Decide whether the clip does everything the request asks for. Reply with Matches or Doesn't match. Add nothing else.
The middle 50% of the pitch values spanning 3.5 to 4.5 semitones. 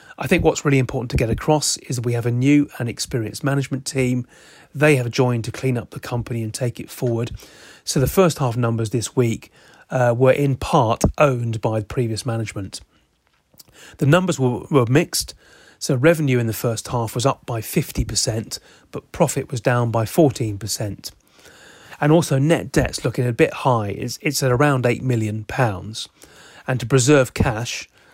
Doesn't match